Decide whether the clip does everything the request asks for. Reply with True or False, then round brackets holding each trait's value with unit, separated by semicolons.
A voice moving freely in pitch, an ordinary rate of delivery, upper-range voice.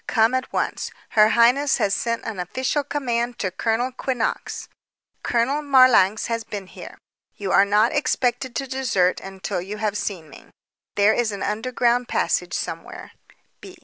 False (3.9 semitones; 150 wpm; 230 Hz)